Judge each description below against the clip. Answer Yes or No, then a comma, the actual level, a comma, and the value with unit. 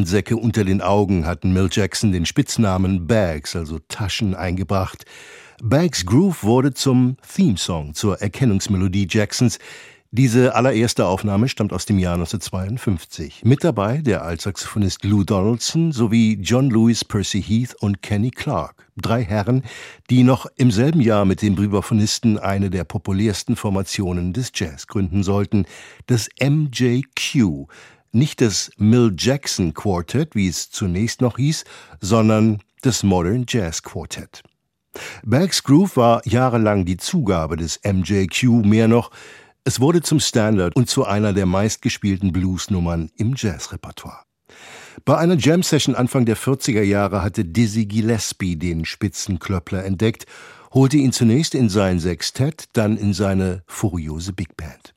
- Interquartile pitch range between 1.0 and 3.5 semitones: No, average, 4.4 semitones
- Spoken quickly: No, average, 140 wpm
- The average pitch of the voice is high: No, low, 110 Hz